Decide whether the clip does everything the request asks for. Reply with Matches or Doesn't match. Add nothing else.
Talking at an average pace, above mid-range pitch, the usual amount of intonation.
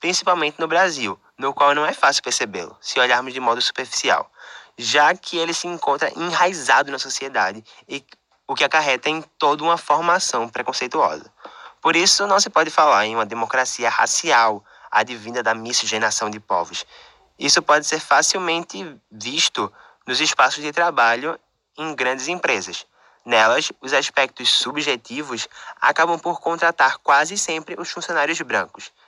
Doesn't match